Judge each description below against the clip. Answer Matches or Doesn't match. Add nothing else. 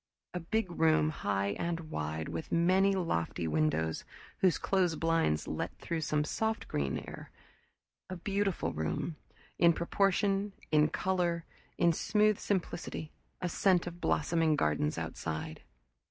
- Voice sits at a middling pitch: Matches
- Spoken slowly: Matches